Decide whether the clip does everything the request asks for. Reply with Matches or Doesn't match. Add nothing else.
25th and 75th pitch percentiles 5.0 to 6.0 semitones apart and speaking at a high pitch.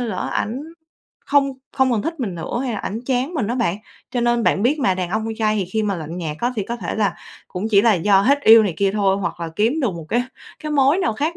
Doesn't match